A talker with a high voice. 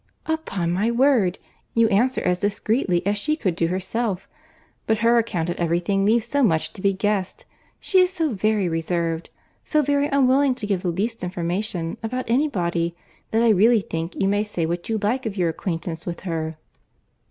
Yes: high, 200 Hz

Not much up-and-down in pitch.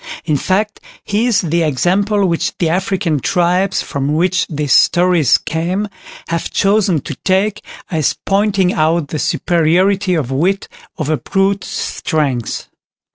No: average, 3.9 semitones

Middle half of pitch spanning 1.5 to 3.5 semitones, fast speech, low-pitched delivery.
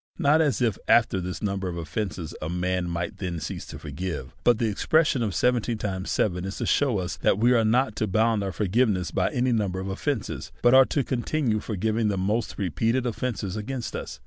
No: average, 4.6 semitones; fast, 220 wpm; low, 105 Hz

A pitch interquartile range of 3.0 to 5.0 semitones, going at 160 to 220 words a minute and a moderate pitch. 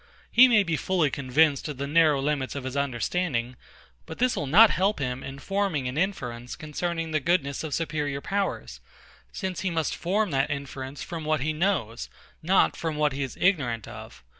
Yes: average, 4.5 semitones; average, 190 wpm; medium, 150 Hz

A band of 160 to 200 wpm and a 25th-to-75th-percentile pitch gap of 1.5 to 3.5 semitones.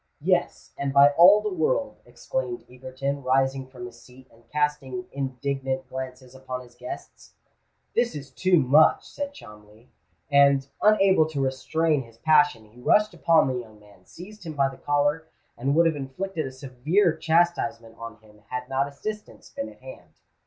No: average, 165 wpm; average, 4.2 semitones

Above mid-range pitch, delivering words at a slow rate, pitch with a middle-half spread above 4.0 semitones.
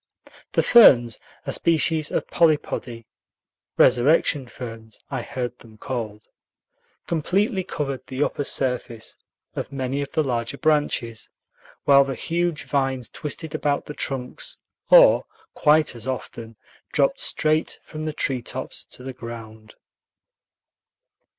No: low, 135 Hz; slow, 120 wpm; average, 4.4 semitones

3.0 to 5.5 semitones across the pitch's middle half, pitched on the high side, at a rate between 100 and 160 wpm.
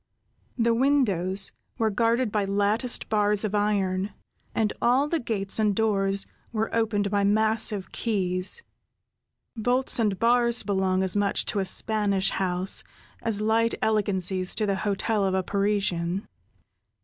No: narrow, 2.6 semitones; high, 205 Hz; slow, 135 wpm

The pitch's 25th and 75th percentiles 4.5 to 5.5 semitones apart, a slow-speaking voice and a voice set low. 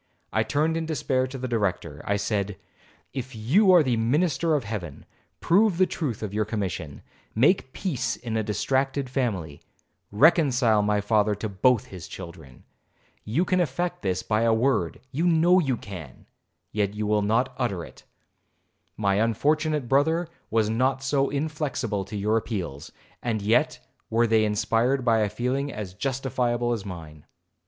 No: average, 5.0 semitones; average, 160 wpm; low, 115 Hz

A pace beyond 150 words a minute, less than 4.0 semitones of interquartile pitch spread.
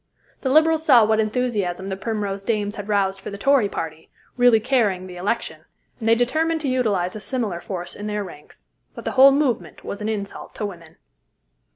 No: average, 195 wpm; average, 4.3 semitones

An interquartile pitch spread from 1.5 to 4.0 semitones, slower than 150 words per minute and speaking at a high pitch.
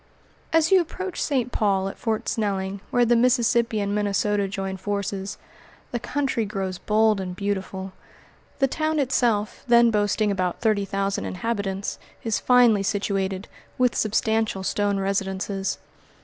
Yes: average, 3.2 semitones; slow, 135 wpm; high, 205 Hz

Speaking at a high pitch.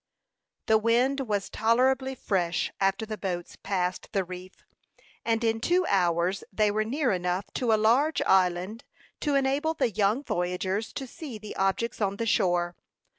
Yes: high, 215 Hz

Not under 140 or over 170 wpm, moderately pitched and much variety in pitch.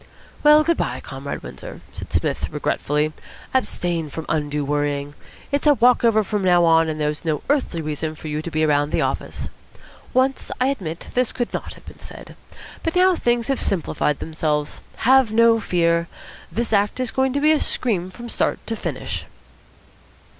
No: average, 180 wpm; medium, 180 Hz; wide, 8.5 semitones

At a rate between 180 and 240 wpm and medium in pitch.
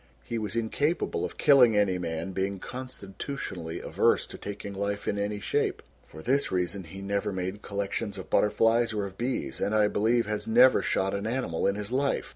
No: average, 190 wpm; low, 105 Hz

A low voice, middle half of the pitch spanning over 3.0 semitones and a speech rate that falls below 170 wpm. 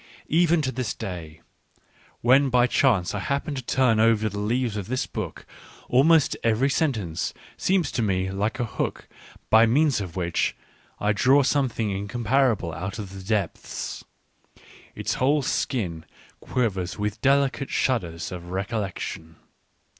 Yes: low, 110 Hz; wide, 5.4 semitones; average, 140 wpm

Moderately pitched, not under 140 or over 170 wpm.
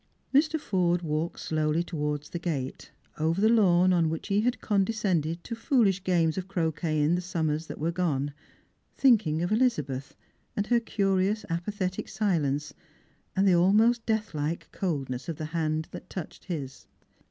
Yes: medium, 175 Hz; average, 165 wpm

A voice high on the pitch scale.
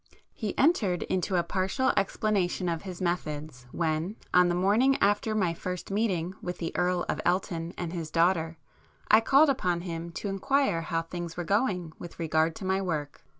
No: medium, 180 Hz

